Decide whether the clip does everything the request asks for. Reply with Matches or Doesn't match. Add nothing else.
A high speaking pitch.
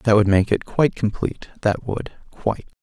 Doesn't match